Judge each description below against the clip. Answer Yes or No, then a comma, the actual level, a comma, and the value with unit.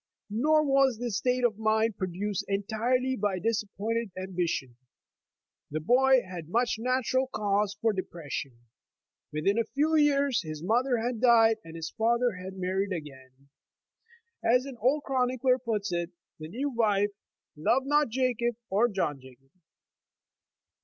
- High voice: Yes, high, 220 Hz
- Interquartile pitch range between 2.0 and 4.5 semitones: No, average, 5.3 semitones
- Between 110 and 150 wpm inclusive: Yes, average, 140 wpm